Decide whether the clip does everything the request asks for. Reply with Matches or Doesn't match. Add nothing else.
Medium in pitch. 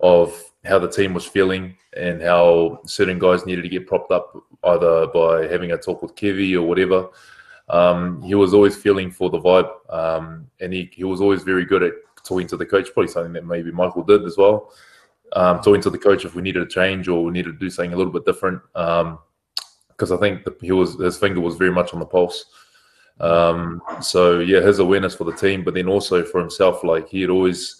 Doesn't match